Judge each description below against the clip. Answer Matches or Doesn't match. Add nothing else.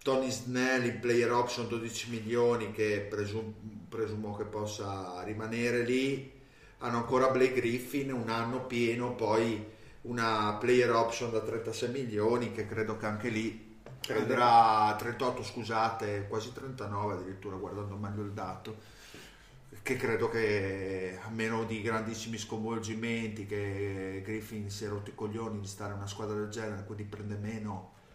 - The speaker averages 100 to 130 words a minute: Doesn't match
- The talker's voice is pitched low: Matches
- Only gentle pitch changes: Matches